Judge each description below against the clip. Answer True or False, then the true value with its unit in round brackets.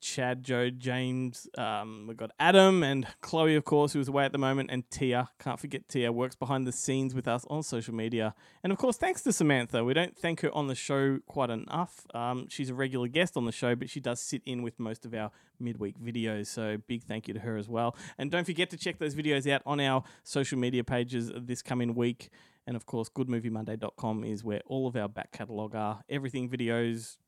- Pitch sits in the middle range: False (125 Hz)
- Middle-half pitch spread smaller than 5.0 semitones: True (3.2 semitones)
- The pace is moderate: False (225 wpm)